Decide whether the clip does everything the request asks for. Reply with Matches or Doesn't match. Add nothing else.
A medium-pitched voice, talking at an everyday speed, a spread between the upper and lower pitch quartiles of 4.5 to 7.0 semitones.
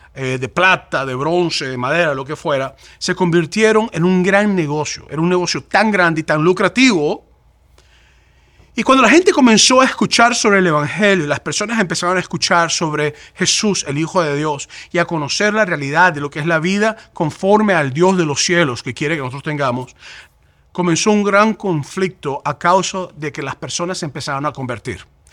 Matches